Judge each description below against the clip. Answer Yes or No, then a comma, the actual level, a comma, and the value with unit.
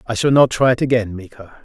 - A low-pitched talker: Yes, low, 115 Hz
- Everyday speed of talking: No, fast, 255 wpm